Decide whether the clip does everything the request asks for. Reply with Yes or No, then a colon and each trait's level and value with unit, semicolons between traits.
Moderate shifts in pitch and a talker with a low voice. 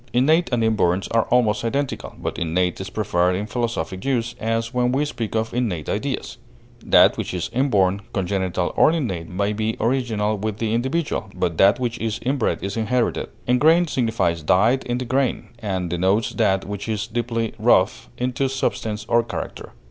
Yes: average, 4.1 semitones; low, 115 Hz